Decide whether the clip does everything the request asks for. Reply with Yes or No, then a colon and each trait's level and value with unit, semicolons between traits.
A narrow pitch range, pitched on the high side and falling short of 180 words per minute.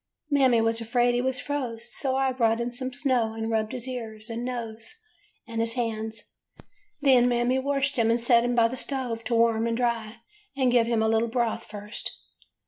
No: narrow, 1.9 semitones; high, 235 Hz; average, 200 wpm